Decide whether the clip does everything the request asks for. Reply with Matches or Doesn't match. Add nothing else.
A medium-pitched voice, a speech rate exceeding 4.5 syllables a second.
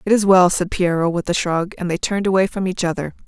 Matches